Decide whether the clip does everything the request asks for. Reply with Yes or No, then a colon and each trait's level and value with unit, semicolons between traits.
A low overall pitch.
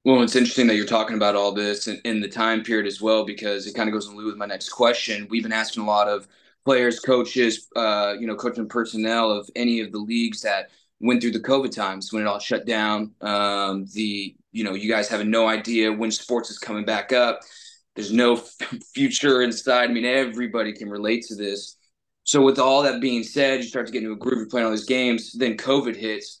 Yes: low, 115 Hz